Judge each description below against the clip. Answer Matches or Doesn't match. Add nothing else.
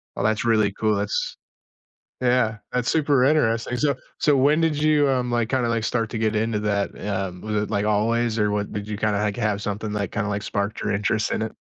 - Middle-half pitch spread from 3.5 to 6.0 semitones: Doesn't match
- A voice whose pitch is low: Matches